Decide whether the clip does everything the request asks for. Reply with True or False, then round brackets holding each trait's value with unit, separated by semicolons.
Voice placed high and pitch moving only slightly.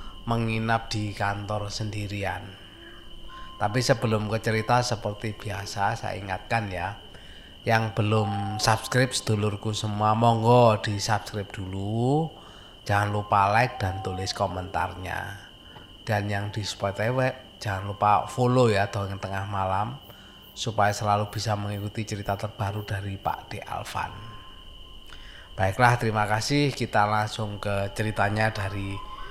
False (105 Hz; 2.0 semitones)